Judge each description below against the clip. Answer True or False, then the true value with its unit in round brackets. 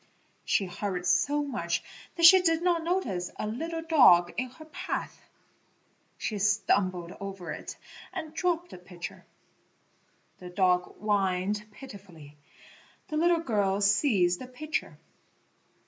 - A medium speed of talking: False (125 wpm)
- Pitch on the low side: False (210 Hz)